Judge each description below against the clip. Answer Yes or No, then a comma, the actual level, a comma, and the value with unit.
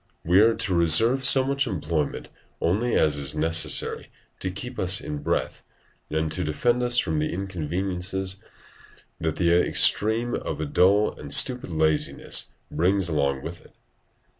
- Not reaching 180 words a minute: Yes, average, 155 wpm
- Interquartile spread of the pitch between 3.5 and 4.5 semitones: No, average, 5.2 semitones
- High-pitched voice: No, very low, 90 Hz